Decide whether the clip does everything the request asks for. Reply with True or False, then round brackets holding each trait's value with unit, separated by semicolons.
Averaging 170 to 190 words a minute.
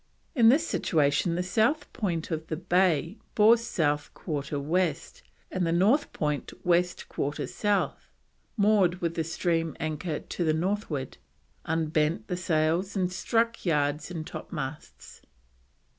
False (135 wpm)